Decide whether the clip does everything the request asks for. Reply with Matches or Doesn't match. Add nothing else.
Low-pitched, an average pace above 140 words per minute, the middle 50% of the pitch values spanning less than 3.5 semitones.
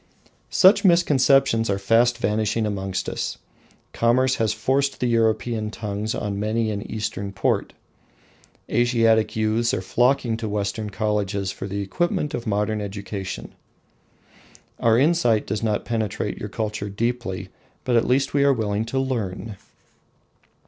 Doesn't match